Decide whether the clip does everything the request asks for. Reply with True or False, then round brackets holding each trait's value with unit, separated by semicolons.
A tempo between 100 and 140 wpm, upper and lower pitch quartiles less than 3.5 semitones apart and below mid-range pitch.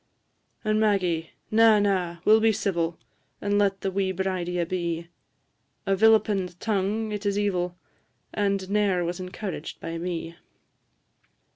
False (135 wpm; 2.7 semitones; 195 Hz)